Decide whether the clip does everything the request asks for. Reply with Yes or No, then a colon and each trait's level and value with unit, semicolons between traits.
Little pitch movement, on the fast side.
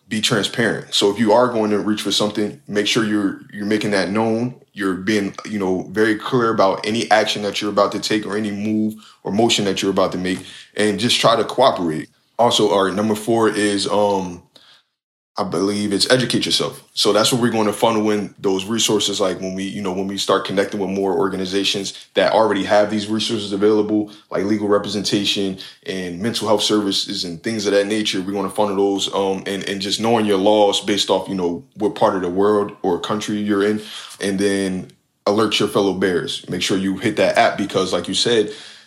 Yes: narrow, 1.5 semitones; fast, 215 wpm